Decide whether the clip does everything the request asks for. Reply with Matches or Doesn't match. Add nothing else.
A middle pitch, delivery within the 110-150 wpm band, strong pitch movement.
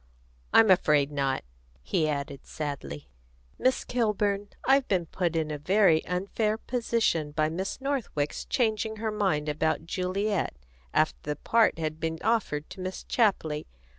Matches